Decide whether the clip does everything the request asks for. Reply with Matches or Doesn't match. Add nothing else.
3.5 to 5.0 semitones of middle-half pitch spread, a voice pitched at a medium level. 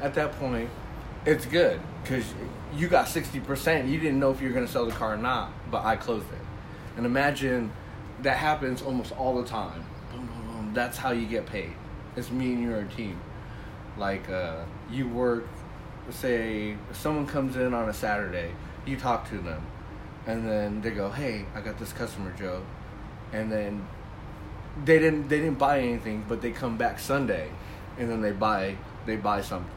Doesn't match